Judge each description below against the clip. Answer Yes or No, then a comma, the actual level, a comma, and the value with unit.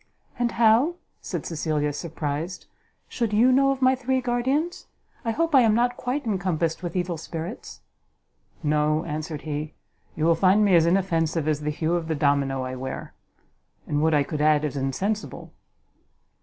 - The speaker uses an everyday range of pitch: No, wide, 7.4 semitones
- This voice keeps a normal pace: Yes, average, 170 wpm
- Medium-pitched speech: Yes, medium, 170 Hz